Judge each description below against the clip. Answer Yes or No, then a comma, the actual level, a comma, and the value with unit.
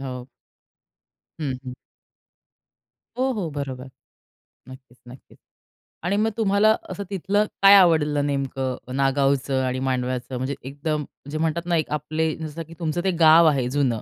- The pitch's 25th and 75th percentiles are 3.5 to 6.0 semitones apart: Yes, average, 4.2 semitones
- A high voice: No, medium, 145 Hz